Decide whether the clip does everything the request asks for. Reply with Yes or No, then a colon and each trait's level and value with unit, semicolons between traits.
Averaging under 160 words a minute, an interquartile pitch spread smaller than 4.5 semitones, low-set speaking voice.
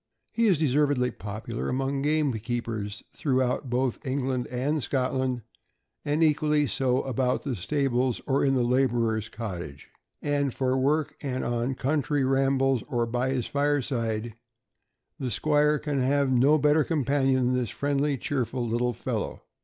Yes: average, 145 wpm; average, 2.8 semitones; low, 130 Hz